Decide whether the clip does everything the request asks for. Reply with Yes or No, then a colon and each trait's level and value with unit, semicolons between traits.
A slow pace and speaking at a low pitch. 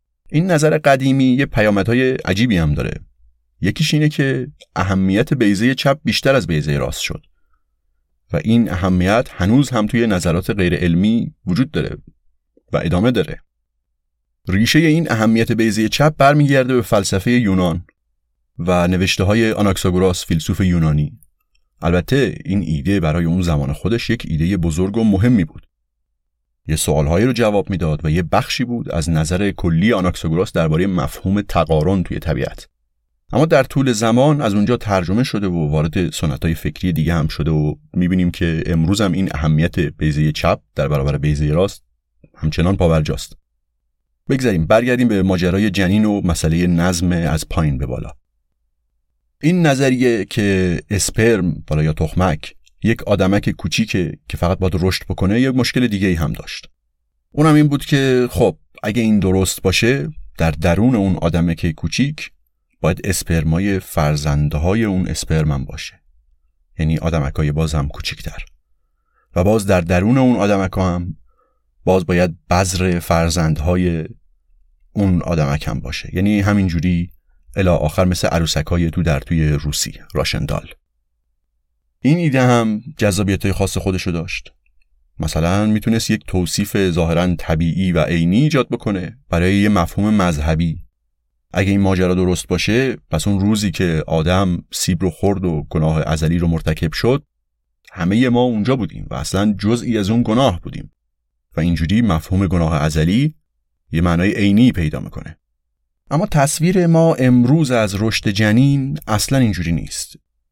No: average, 150 wpm; very low, 90 Hz